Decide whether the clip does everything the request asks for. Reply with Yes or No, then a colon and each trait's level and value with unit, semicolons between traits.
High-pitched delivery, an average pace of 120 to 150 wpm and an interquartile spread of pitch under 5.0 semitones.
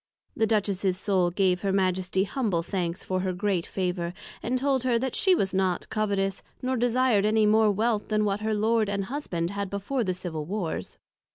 No: high, 200 Hz; average, 190 wpm; average, 3.1 semitones